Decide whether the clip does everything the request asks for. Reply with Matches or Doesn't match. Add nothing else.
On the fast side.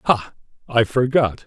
Doesn't match